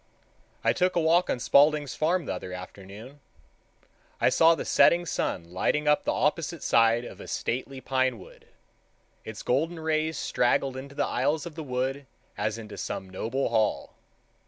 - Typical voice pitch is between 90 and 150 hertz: Yes, low, 135 Hz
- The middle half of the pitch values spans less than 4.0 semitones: No, average, 5.2 semitones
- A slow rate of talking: No, average, 165 wpm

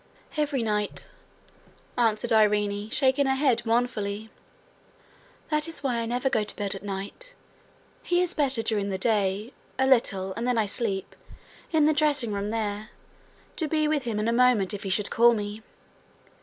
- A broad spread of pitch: No, average, 4.4 semitones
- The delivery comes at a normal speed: Yes, average, 170 wpm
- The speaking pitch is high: Yes, high, 230 Hz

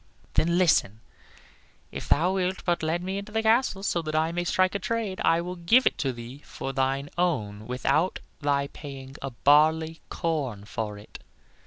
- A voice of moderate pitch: Yes, medium, 160 Hz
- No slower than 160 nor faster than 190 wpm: Yes, average, 180 wpm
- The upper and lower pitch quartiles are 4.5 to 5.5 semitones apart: Yes, average, 5.2 semitones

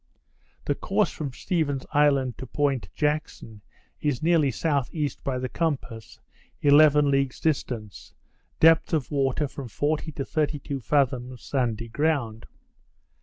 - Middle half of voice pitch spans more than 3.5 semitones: No, average, 3.0 semitones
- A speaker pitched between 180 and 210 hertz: No, medium, 140 Hz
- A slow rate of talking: Yes, slow, 125 wpm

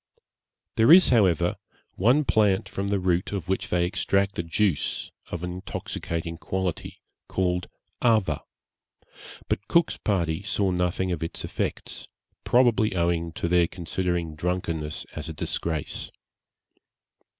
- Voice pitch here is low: Yes, very low, 90 Hz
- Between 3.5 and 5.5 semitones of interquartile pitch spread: No, average, 2.9 semitones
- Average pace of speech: No, slow, 130 wpm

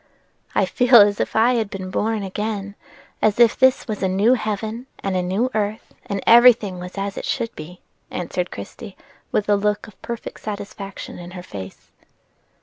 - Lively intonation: No, average, 2.9 semitones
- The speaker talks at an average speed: Yes, average, 185 wpm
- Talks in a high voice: Yes, high, 205 Hz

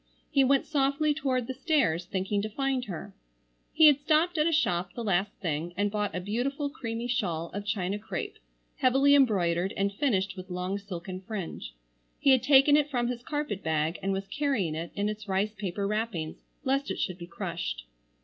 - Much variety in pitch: Yes, wide, 6.7 semitones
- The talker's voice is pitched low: No, high, 210 Hz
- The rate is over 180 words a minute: Yes, average, 190 wpm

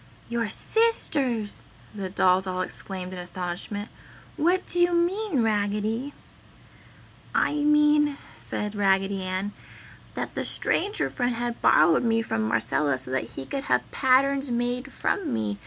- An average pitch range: No, wide, 7.2 semitones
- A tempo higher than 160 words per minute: No, average, 140 wpm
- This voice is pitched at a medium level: No, high, 225 Hz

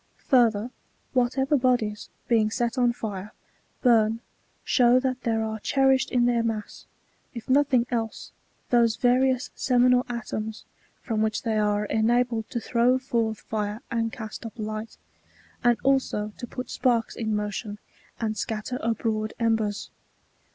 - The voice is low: No, high, 230 Hz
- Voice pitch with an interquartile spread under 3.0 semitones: Yes, narrow, 2.4 semitones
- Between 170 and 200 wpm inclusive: No, slow, 135 wpm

